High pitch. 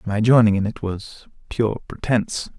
No: low, 110 Hz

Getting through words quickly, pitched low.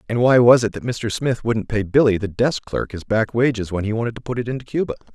Yes: fast, 280 wpm; low, 115 Hz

